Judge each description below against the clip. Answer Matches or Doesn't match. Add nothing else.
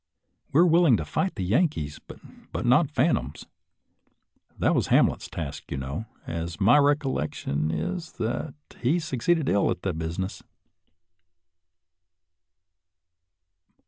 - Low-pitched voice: Matches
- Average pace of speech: Doesn't match